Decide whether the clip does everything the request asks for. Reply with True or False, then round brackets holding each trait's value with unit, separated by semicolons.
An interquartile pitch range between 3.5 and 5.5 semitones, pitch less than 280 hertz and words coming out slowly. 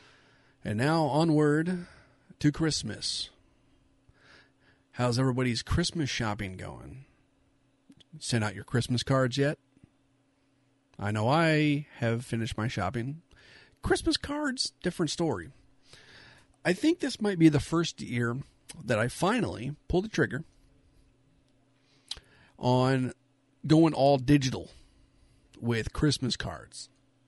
True (4.6 semitones; 135 Hz; 105 wpm)